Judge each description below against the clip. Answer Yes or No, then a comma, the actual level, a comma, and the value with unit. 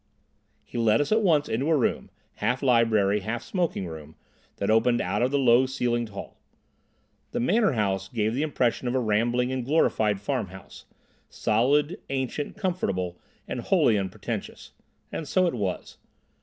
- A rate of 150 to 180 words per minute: Yes, average, 155 wpm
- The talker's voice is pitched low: Yes, low, 120 Hz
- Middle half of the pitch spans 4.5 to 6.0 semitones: Yes, average, 4.8 semitones